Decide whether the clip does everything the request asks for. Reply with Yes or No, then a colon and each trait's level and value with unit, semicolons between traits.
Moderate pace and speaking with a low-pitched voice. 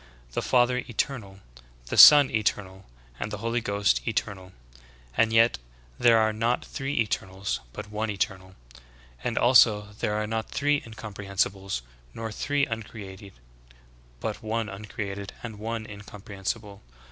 No: slow, 130 wpm; low, 105 Hz